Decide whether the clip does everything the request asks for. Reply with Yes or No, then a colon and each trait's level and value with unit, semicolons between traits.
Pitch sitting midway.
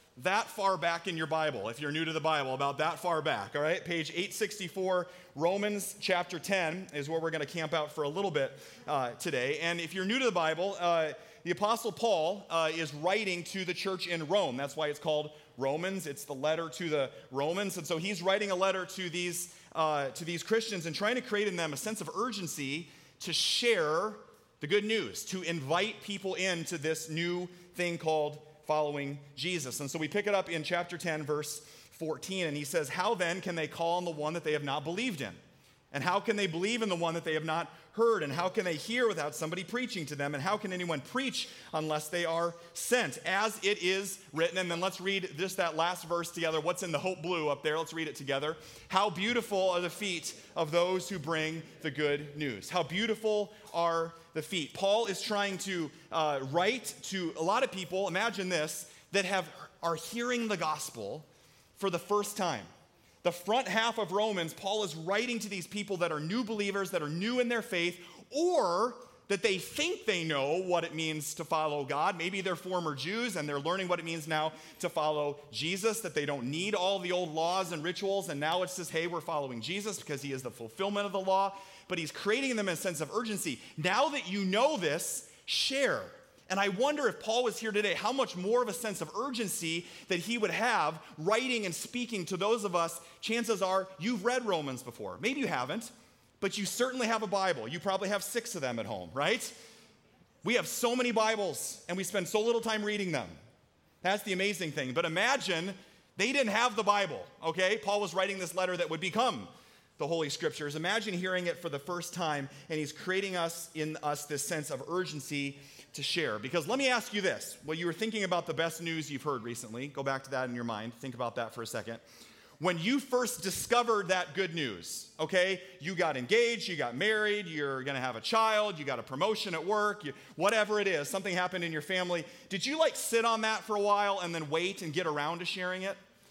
Yes: medium, 180 Hz